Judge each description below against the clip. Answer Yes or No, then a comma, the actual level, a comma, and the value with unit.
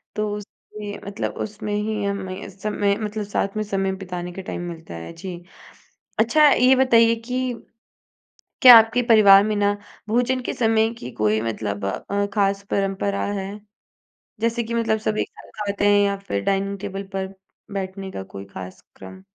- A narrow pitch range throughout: Yes, narrow, 2.3 semitones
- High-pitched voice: Yes, high, 200 Hz